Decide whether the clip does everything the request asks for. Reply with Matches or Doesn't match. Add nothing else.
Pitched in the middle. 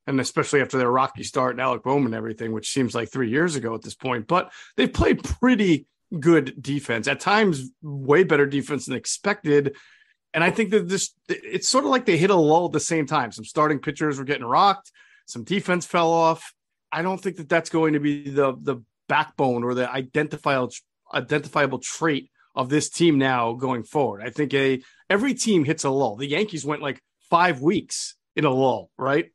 Matches